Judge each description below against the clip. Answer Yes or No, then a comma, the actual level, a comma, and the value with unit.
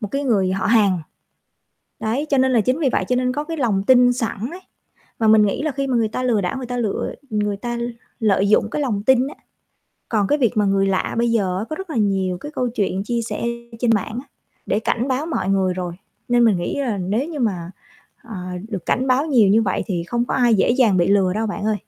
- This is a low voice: No, high, 225 Hz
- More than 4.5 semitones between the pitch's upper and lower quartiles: No, average, 4.2 semitones